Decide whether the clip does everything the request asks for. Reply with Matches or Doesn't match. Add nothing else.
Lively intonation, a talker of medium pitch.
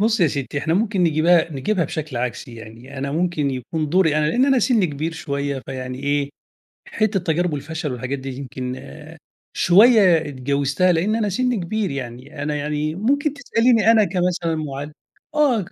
Matches